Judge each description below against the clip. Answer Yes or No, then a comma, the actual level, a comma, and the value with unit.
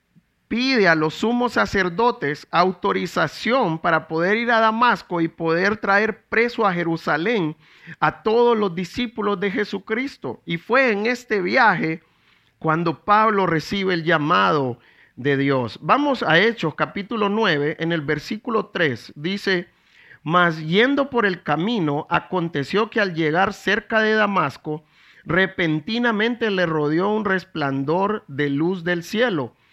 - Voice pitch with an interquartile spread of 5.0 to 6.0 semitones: Yes, wide, 5.4 semitones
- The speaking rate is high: No, slow, 135 wpm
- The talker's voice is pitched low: No, medium, 185 Hz